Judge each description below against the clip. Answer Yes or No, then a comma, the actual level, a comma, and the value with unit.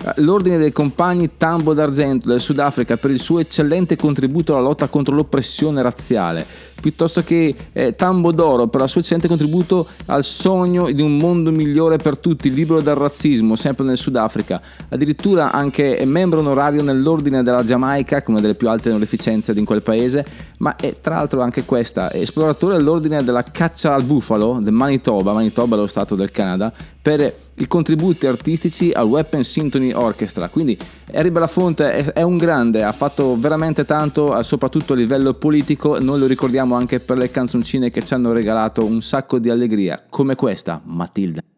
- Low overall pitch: No, medium, 145 Hz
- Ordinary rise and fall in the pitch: Yes, average, 4.5 semitones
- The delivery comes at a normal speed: No, fast, 175 wpm